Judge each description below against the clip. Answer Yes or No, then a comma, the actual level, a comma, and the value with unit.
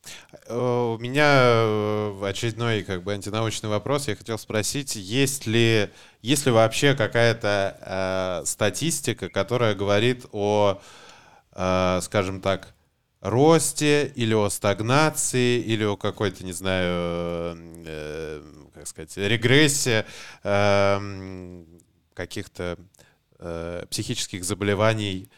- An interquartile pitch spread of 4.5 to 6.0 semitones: No, average, 4.0 semitones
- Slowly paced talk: Yes, slow, 95 wpm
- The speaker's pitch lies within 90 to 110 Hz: Yes, low, 105 Hz